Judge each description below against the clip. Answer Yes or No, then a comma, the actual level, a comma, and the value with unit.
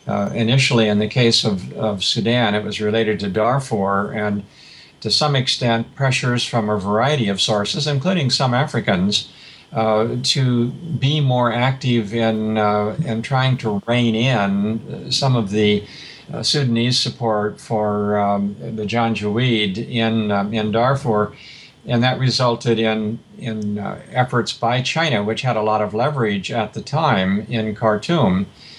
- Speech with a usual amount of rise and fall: Yes, average, 3.4 semitones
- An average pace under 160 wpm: Yes, average, 150 wpm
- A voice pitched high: No, low, 115 Hz